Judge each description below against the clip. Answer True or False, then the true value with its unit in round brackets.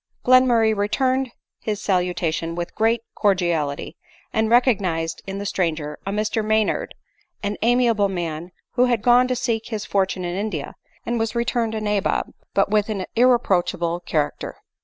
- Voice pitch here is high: True (210 Hz)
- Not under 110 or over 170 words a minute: True (150 wpm)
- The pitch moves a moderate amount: True (4.6 semitones)